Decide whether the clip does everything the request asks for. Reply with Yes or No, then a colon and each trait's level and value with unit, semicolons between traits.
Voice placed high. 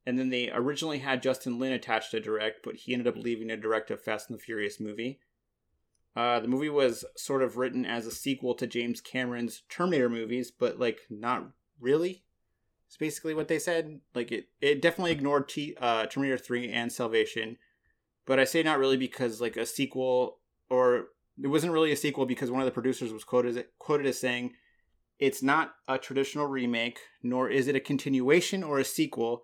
No: low, 130 Hz